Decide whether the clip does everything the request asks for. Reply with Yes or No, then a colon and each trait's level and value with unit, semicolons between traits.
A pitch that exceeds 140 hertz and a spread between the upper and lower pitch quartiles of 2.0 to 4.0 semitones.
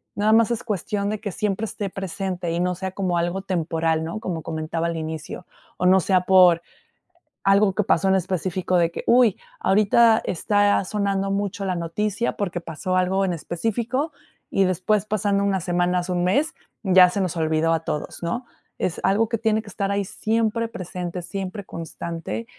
Yes: high, 190 Hz; average, 2.9 semitones